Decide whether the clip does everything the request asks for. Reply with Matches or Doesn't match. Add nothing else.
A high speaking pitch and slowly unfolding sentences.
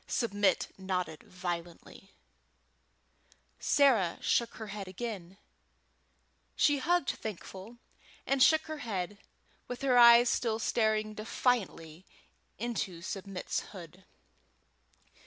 Matches